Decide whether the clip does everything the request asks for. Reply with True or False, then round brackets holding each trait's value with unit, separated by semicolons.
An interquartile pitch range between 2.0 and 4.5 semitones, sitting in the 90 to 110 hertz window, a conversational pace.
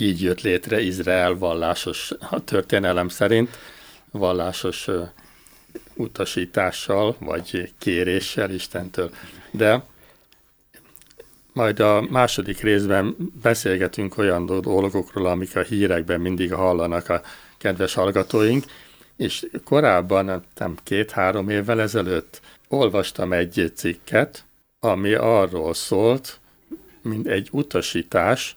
False (2.9 semitones; 95 Hz; 90 wpm)